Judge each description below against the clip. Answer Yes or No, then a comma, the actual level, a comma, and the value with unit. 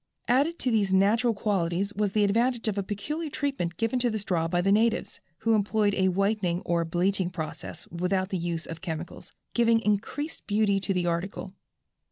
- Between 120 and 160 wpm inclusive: No, average, 185 wpm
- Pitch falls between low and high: No, high, 200 Hz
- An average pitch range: Yes, average, 4.0 semitones